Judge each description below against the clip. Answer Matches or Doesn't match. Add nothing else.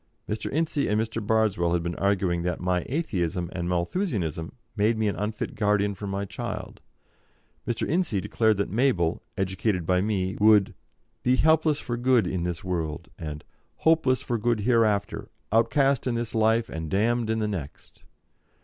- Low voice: Matches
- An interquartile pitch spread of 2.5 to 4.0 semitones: Doesn't match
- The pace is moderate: Matches